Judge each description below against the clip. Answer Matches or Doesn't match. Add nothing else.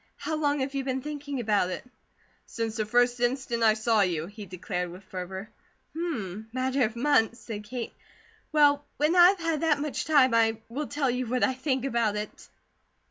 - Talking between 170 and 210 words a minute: Matches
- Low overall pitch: Doesn't match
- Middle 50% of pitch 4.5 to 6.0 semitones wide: Matches